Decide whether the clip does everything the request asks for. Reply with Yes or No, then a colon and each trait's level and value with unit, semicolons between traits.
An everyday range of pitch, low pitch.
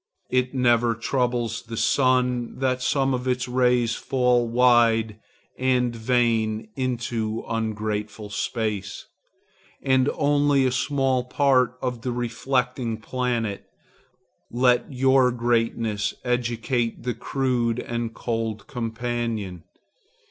No: narrow, 1.9 semitones; low, 120 Hz